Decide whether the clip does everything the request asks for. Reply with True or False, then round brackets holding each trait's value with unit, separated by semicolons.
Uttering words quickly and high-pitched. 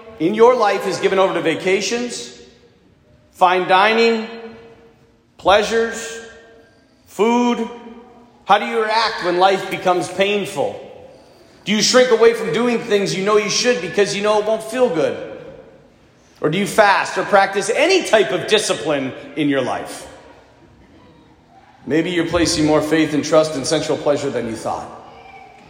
False (150 wpm; 205 Hz)